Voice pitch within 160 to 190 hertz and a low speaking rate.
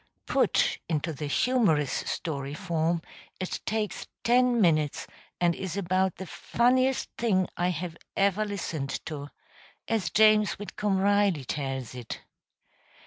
Yes: medium, 185 Hz; slow, 125 wpm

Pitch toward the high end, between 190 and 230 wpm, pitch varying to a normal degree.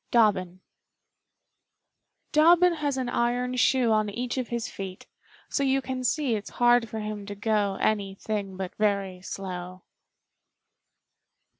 No: high, 215 Hz; slow, 135 wpm; average, 4.1 semitones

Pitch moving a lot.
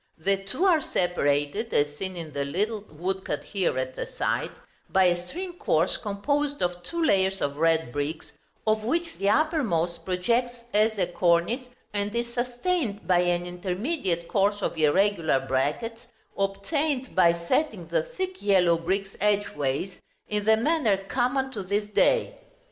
Yes: wide, 5.8 semitones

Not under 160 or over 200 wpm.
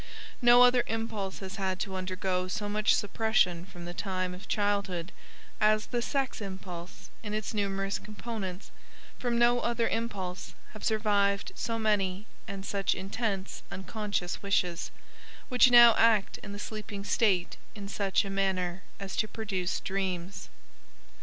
No: average, 145 wpm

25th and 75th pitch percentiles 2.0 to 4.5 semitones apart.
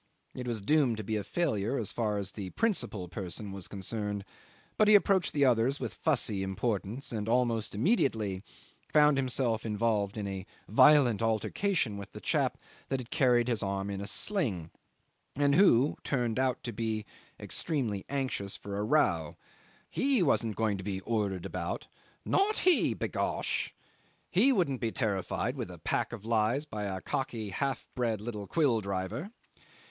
No: average, 5.3 semitones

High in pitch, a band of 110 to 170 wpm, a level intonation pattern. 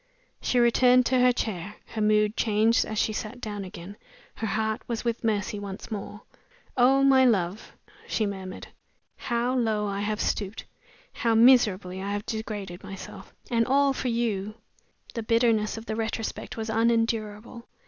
Yes: high, 220 Hz; average, 160 wpm; narrow, 2.3 semitones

